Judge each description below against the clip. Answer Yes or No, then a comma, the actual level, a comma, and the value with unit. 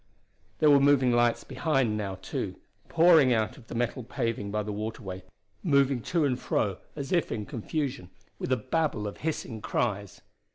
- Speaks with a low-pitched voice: Yes, low, 120 Hz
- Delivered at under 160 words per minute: No, average, 170 wpm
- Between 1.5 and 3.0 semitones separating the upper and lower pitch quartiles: No, average, 4.8 semitones